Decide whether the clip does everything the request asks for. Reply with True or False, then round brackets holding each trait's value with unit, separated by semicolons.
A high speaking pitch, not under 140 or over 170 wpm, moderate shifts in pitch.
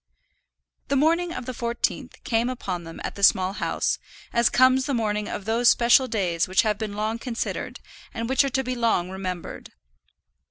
False (230 Hz; 185 wpm; 4.2 semitones)